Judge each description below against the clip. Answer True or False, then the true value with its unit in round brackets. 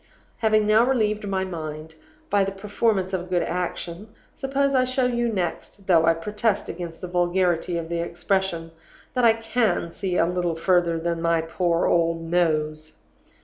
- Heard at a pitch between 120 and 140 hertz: False (180 Hz)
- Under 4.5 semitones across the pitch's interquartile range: True (4.0 semitones)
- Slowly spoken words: False (170 wpm)